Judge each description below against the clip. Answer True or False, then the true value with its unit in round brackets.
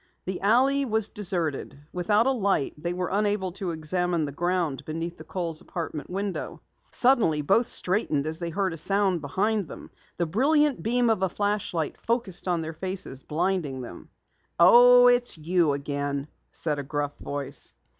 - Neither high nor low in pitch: True (180 Hz)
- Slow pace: False (165 wpm)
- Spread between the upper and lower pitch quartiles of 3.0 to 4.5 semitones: False (4.9 semitones)